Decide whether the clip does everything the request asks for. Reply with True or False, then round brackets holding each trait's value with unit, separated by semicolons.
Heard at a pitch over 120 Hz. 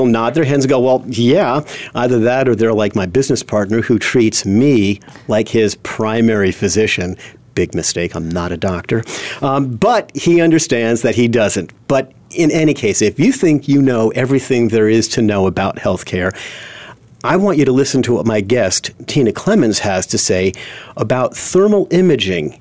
False (115 Hz)